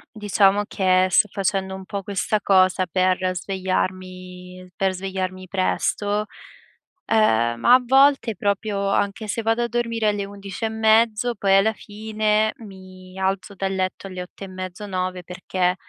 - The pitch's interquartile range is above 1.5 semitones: Yes, narrow, 2.4 semitones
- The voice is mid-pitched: No, high, 195 Hz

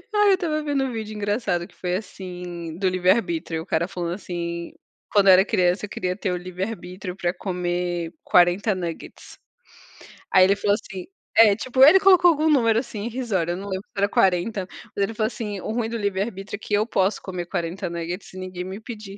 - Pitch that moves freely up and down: No, average, 3.7 semitones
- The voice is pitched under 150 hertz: No, high, 195 Hz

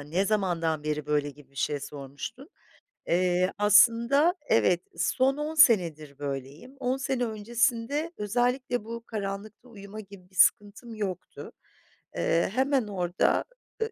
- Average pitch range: No, wide, 6.5 semitones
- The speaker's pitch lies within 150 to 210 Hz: Yes, high, 205 Hz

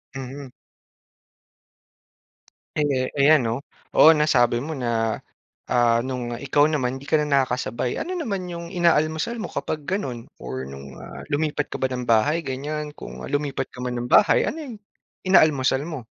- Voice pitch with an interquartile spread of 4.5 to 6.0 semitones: No, average, 4.0 semitones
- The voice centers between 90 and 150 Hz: Yes, medium, 140 Hz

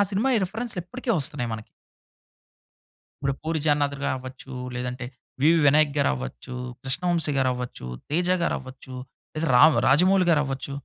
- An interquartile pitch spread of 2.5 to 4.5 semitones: No, average, 4.9 semitones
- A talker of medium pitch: Yes, medium, 145 Hz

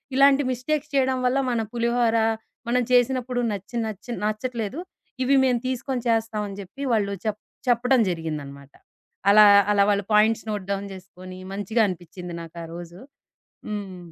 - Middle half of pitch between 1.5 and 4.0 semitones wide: No, average, 4.7 semitones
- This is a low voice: No, high, 220 Hz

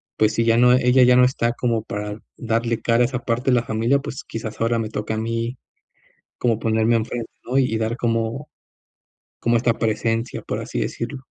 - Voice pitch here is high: No, low, 115 Hz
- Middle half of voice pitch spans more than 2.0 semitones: No, narrow, 1.6 semitones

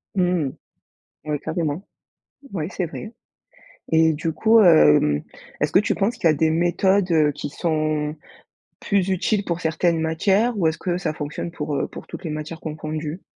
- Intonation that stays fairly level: No, average, 3.1 semitones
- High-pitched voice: No, medium, 160 Hz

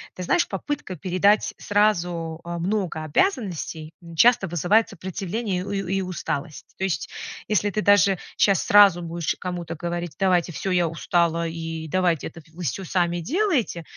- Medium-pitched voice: Yes, medium, 180 Hz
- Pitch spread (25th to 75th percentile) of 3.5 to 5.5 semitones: No, average, 3.1 semitones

